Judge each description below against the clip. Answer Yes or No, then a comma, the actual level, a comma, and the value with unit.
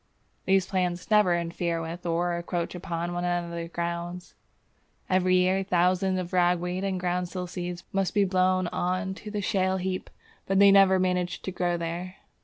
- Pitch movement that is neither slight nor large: No, narrow, 1.3 semitones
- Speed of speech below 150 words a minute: No, average, 165 wpm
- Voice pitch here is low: No, medium, 180 Hz